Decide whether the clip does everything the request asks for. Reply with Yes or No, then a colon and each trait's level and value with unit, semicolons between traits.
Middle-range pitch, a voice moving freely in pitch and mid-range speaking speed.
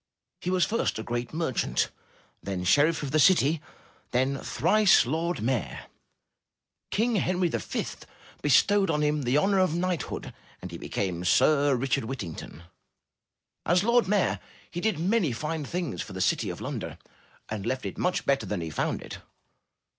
Yes: medium, 150 Hz; wide, 6.8 semitones; average, 160 wpm